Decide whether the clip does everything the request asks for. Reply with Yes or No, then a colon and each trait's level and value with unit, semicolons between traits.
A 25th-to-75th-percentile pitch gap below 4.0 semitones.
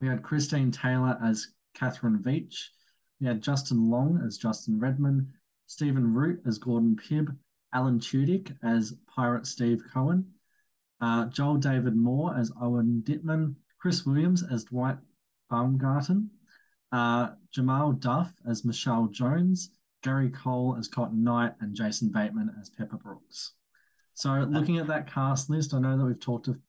No: average, 4.3 semitones